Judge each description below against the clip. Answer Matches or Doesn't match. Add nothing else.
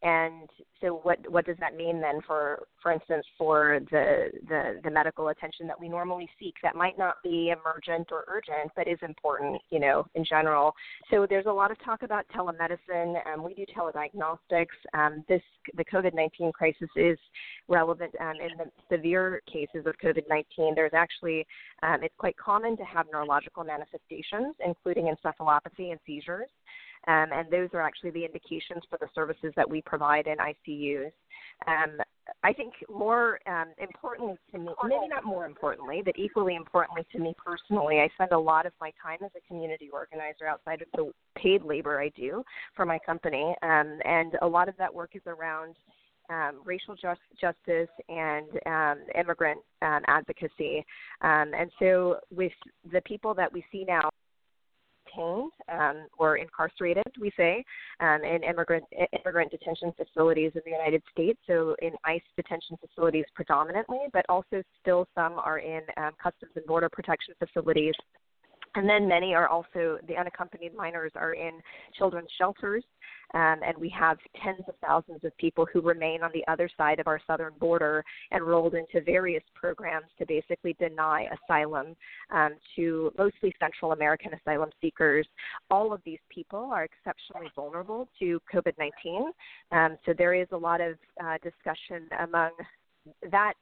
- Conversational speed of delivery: Matches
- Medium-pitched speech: Matches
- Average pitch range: Doesn't match